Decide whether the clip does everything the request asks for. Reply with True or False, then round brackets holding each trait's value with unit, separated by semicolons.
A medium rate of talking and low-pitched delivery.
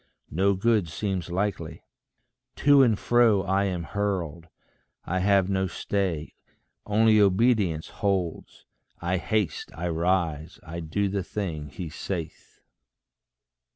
False (120 wpm; 95 Hz)